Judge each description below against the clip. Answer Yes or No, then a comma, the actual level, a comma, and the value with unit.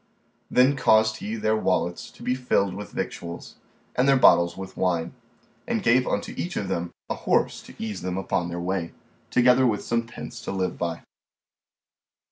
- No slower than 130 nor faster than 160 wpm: No, average, 175 wpm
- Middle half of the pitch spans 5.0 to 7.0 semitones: Yes, average, 5.3 semitones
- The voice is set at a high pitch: No, low, 100 Hz